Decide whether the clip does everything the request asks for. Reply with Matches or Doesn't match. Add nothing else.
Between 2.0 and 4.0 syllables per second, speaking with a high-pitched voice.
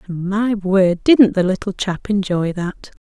Matches